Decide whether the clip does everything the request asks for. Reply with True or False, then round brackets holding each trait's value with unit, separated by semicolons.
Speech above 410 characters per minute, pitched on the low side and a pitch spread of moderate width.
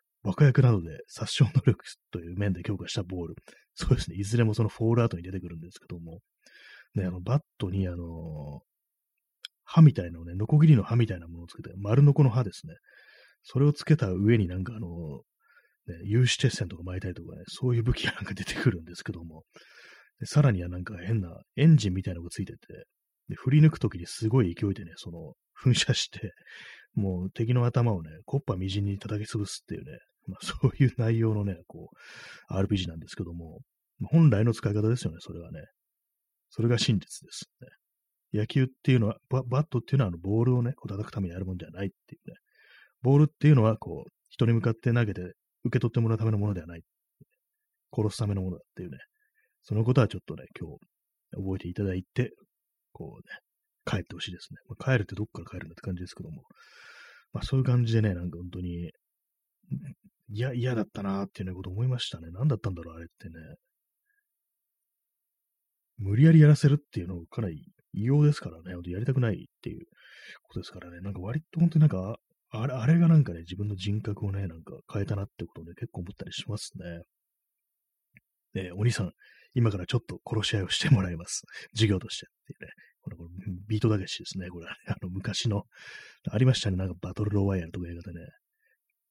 False (420 characters per minute; 105 Hz; 5.7 semitones)